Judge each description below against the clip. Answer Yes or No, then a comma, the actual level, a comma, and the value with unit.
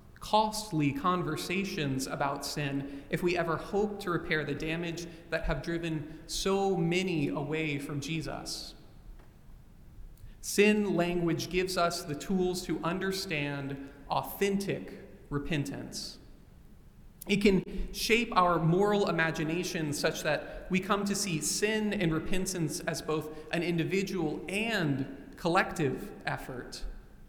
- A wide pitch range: No, average, 3.6 semitones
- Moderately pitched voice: Yes, medium, 165 Hz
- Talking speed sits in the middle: No, slow, 115 wpm